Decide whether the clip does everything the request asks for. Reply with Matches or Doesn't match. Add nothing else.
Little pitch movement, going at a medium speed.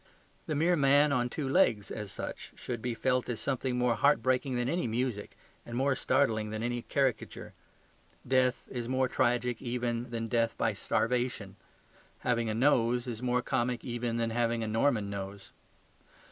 Matches